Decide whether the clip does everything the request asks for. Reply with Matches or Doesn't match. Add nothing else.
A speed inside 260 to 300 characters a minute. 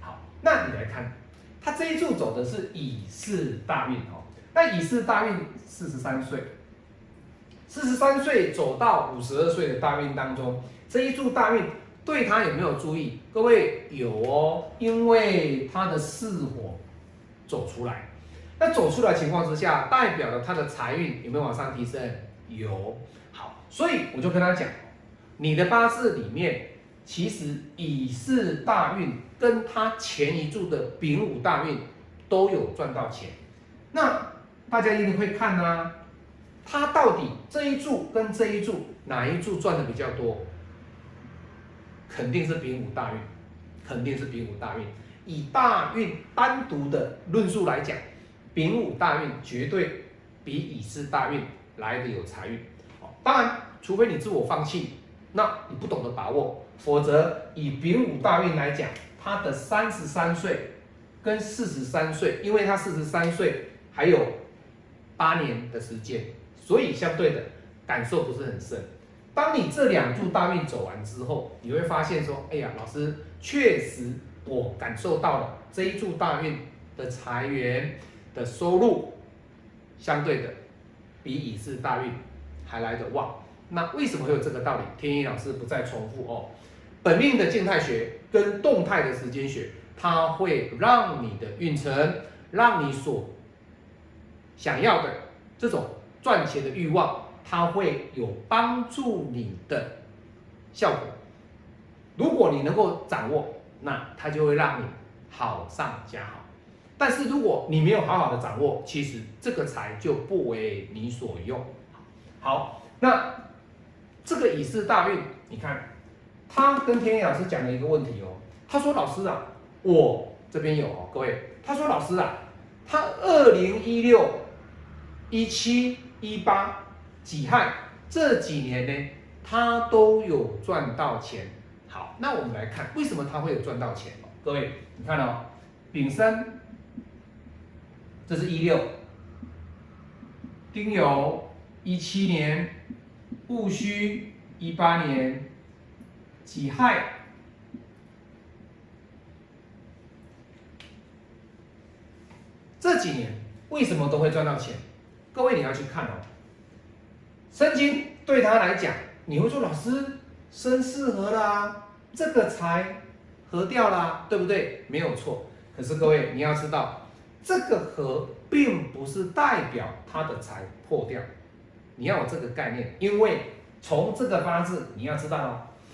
Doesn't match